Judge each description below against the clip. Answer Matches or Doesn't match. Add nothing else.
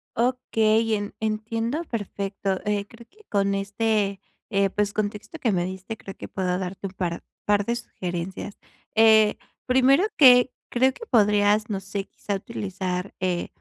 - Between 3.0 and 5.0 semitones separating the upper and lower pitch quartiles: Doesn't match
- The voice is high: Matches